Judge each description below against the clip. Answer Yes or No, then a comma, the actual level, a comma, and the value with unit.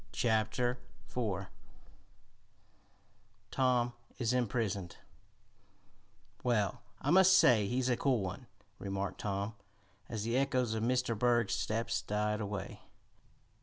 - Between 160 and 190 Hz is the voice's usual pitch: No, low, 115 Hz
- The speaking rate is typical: No, slow, 105 wpm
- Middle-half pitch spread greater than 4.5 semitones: No, average, 3.3 semitones